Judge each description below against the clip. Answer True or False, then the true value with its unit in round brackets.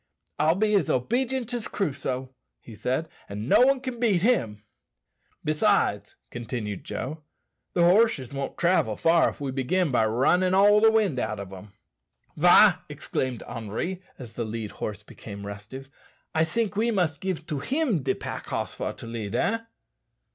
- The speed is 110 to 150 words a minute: False (165 wpm)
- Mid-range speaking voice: True (150 Hz)